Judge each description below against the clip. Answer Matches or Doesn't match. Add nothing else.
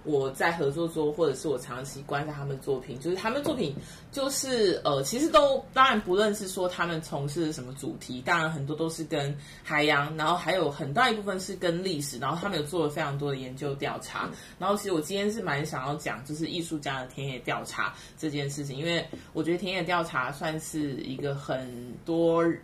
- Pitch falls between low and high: Matches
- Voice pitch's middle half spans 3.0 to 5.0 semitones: Matches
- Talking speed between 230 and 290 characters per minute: Doesn't match